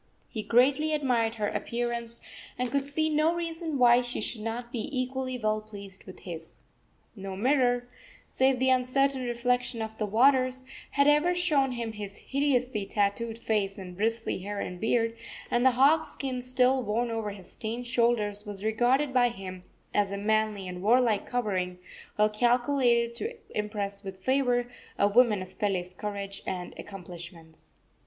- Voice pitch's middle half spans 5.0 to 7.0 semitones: No, average, 3.8 semitones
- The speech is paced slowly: No, average, 160 wpm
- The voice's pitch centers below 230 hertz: No, high, 235 Hz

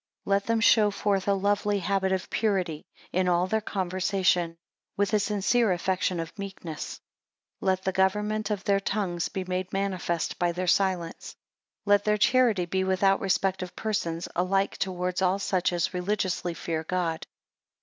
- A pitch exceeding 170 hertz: Yes, high, 190 Hz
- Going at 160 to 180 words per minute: Yes, average, 170 wpm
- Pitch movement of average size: No, narrow, 2.0 semitones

